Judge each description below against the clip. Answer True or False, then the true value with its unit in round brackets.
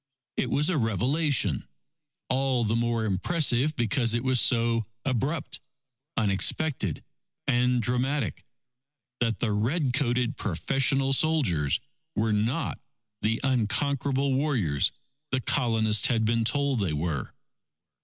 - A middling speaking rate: False (115 wpm)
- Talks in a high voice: False (120 Hz)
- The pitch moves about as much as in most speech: True (3.7 semitones)